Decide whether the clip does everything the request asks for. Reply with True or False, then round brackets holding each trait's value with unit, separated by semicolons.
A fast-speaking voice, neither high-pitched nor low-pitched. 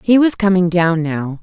True (210 wpm; 180 Hz)